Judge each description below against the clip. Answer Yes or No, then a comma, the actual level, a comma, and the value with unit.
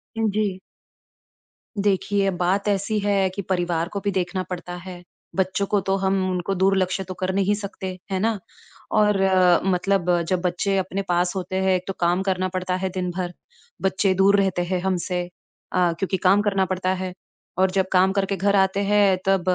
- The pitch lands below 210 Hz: Yes, high, 190 Hz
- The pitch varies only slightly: Yes, narrow, 1.3 semitones